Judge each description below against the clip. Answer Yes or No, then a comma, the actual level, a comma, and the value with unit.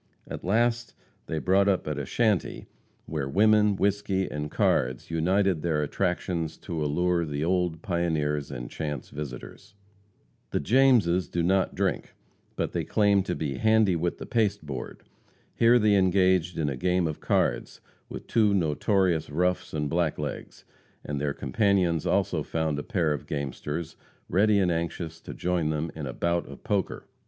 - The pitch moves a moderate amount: Yes, average, 4.6 semitones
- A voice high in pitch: No, very low, 85 Hz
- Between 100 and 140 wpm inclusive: No, average, 160 wpm